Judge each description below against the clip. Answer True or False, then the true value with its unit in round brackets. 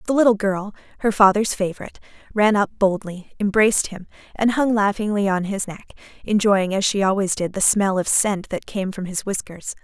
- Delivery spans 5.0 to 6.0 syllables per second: True (5.3 syllables/s)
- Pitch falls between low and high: False (200 Hz)